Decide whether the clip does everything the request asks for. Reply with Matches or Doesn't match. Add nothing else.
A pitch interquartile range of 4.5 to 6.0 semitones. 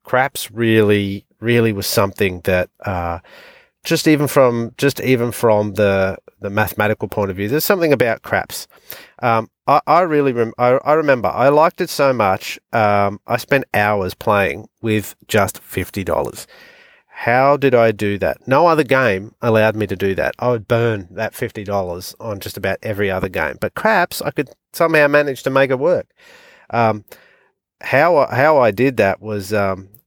Matches